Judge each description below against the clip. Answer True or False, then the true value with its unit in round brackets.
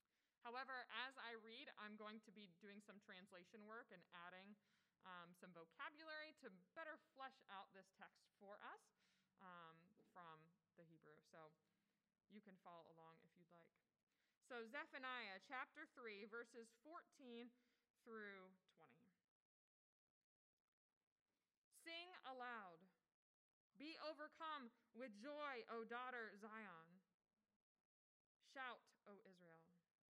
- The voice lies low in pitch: False (215 Hz)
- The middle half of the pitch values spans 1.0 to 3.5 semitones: False (5.0 semitones)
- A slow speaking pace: True (115 wpm)